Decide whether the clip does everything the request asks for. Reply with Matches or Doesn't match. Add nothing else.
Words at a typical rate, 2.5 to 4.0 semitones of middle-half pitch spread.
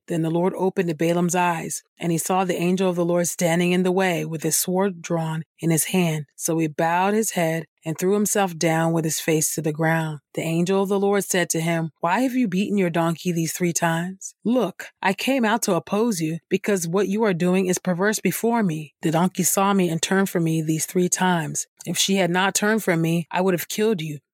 Doesn't match